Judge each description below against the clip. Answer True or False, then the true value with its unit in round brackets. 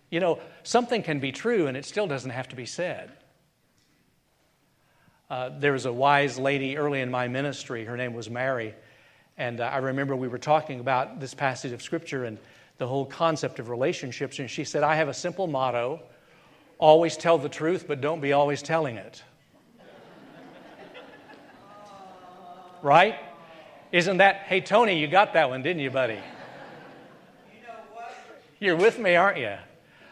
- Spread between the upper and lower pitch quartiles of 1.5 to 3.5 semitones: False (5.2 semitones)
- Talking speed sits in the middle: True (160 wpm)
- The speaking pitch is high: False (145 Hz)